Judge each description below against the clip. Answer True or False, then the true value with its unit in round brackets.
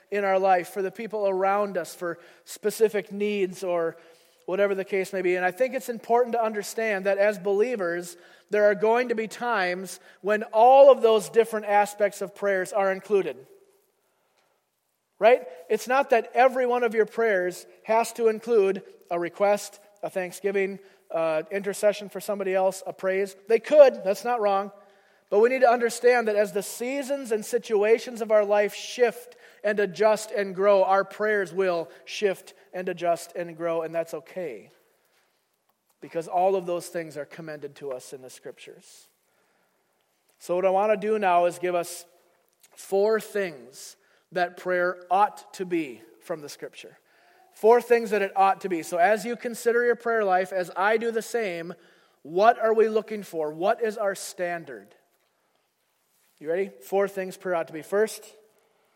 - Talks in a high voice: True (200 Hz)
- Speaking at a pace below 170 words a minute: False (175 wpm)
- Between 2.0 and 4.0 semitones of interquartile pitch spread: True (3.5 semitones)